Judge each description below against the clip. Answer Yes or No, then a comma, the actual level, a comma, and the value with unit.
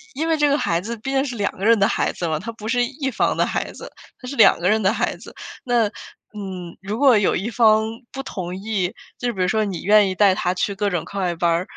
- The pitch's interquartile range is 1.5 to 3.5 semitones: No, average, 4.4 semitones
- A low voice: No, high, 210 Hz